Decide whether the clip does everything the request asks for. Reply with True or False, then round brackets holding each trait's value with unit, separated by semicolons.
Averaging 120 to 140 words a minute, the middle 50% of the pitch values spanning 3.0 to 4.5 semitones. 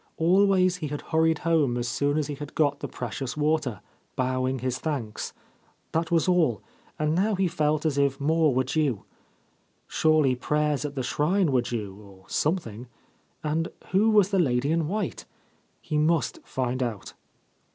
False (165 wpm; 4.2 semitones)